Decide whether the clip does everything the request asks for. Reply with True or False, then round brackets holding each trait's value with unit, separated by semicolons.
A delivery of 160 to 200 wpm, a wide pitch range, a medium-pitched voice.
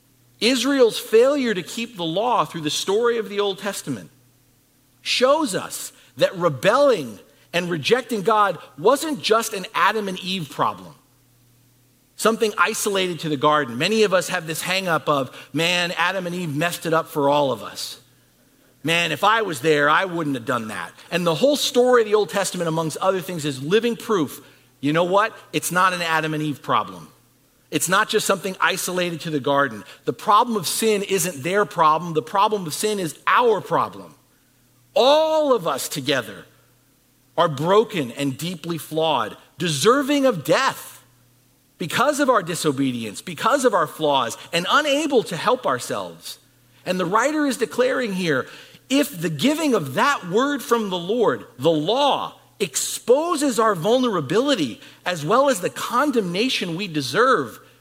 True (165 wpm; 6.9 semitones; 180 Hz)